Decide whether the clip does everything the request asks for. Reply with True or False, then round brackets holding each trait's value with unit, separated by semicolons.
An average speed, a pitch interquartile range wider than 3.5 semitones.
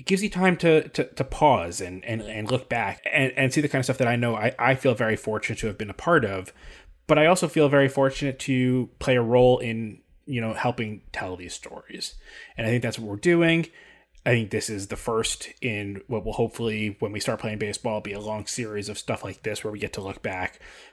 False (250 wpm; 3.9 semitones)